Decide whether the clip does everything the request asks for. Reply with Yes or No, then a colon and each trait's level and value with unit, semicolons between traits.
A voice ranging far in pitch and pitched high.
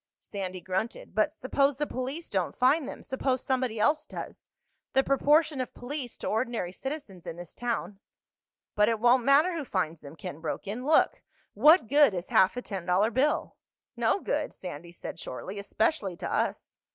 Yes: wide, 6.6 semitones; high, 240 Hz